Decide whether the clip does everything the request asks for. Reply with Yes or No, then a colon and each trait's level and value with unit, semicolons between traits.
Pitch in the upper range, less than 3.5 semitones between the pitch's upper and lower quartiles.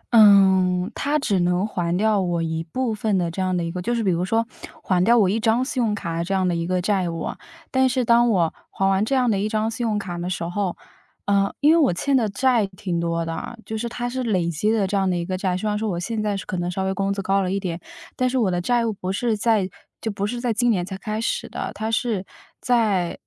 No: high, 200 Hz; average, 3.9 semitones